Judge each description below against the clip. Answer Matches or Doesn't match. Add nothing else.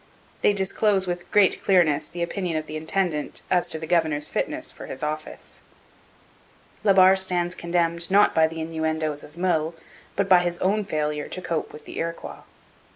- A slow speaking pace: Doesn't match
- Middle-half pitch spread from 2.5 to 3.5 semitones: Matches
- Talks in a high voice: Doesn't match